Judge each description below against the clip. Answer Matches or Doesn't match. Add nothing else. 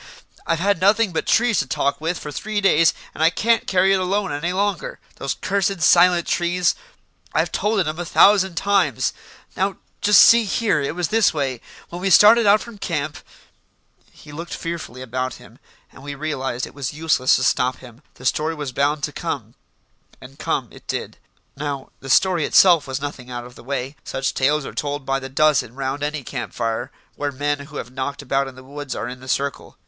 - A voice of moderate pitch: Matches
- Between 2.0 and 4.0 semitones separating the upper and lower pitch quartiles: Doesn't match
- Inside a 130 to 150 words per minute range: Doesn't match